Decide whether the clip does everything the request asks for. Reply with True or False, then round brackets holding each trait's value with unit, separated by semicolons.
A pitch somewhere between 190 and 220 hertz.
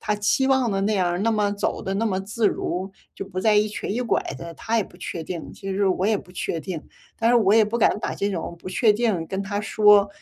True (205 Hz)